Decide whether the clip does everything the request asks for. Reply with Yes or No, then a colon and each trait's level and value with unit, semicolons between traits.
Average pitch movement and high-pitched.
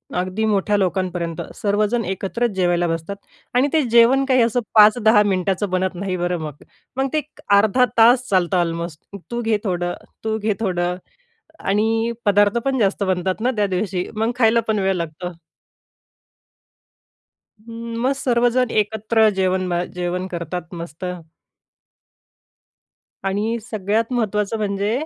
Yes: average, 3.9 semitones; high, 205 Hz